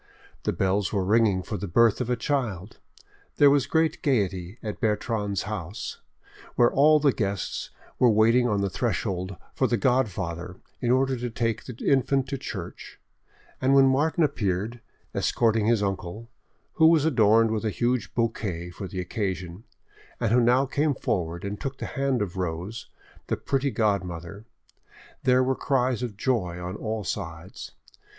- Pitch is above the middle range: No, low, 110 Hz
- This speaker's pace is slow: No, average, 160 wpm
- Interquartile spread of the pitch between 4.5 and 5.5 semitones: Yes, average, 4.9 semitones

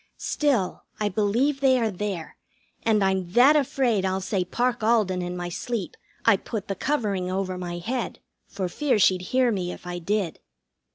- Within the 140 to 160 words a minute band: No, average, 175 wpm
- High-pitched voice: Yes, high, 200 Hz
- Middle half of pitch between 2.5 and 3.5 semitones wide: No, average, 4.7 semitones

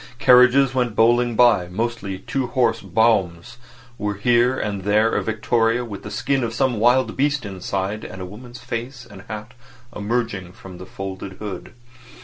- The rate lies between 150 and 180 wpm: Yes, average, 160 wpm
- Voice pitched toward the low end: Yes, low, 115 Hz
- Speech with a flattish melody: No, average, 3.5 semitones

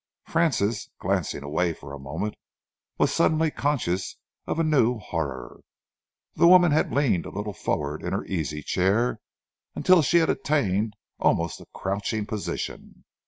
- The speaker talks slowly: No, average, 145 wpm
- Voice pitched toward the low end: Yes, low, 105 Hz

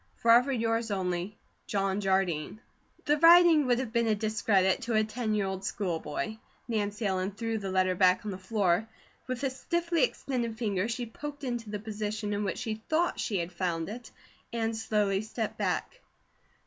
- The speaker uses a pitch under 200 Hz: No, high, 215 Hz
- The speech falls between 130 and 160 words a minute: No, average, 180 wpm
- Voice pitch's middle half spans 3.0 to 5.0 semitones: Yes, average, 3.5 semitones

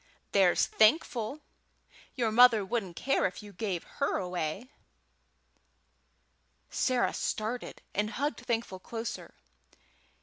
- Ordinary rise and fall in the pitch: Yes, average, 4.2 semitones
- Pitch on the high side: Yes, high, 220 Hz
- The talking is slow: Yes, slow, 100 wpm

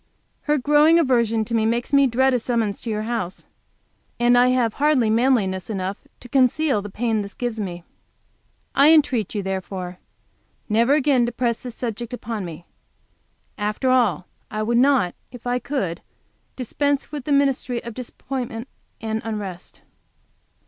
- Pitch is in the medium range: No, high, 235 Hz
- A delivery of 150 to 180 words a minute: Yes, average, 155 wpm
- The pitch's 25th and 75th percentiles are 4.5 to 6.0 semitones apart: No, average, 3.5 semitones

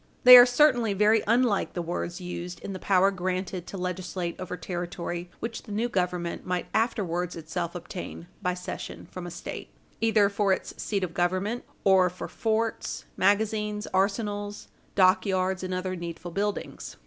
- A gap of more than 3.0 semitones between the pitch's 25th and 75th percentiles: No, average, 2.7 semitones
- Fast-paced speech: No, average, 160 wpm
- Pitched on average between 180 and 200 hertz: Yes, medium, 185 Hz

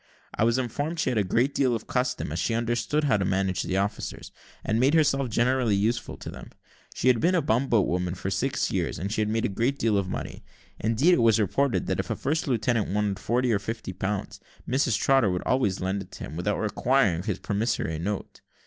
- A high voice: No, low, 110 Hz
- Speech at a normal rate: No, fast, 220 wpm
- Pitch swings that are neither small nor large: Yes, average, 4.6 semitones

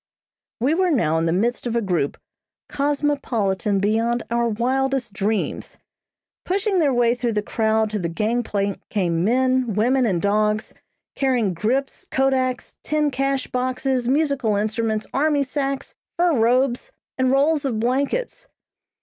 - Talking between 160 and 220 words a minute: No, average, 140 wpm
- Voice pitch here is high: Yes, high, 245 Hz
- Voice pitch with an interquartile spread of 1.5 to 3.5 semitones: No, average, 4.2 semitones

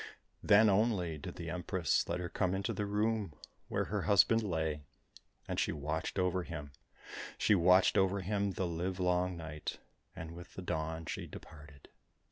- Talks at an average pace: Yes, average, 165 wpm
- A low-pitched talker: Yes, very low, 90 Hz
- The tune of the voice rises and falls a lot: No, average, 3.3 semitones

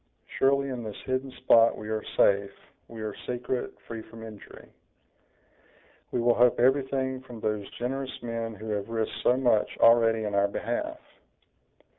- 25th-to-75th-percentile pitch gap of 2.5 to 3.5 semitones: Yes, average, 2.9 semitones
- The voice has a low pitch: Yes, low, 115 Hz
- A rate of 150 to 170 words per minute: Yes, average, 155 wpm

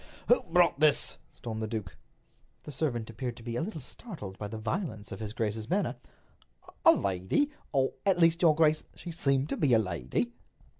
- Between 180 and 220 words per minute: Yes, average, 185 wpm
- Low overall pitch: Yes, low, 125 Hz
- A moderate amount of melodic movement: No, wide, 7.0 semitones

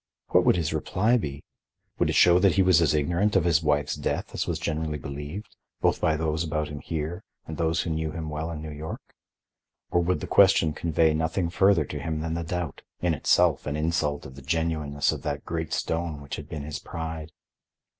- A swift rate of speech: Yes, fast, 210 wpm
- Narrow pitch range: Yes, narrow, 2.0 semitones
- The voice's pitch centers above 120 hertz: No, very low, 80 Hz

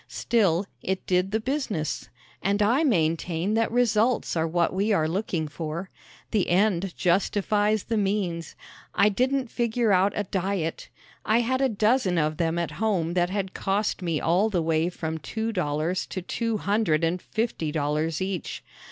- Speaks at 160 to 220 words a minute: Yes, average, 165 wpm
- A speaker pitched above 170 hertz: Yes, high, 190 Hz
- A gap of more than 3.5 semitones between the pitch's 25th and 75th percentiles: Yes, average, 4.5 semitones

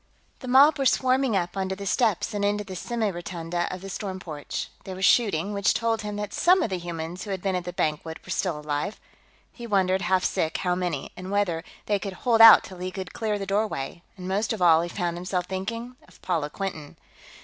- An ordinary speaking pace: No, fast, 230 wpm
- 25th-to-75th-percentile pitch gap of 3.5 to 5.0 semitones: No, average, 3.1 semitones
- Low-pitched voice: No, high, 190 Hz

